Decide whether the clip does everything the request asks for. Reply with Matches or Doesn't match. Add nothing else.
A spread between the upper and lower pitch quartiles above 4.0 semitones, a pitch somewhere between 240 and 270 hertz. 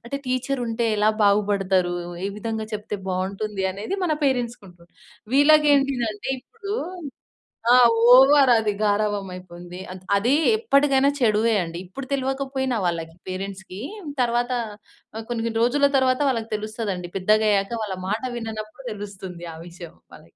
Doesn't match